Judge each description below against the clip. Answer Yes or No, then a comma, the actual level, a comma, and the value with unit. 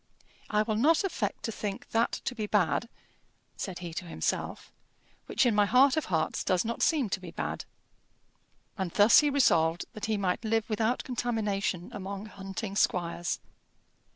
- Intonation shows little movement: No, average, 3.8 semitones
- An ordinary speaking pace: Yes, average, 165 wpm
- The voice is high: Yes, high, 210 Hz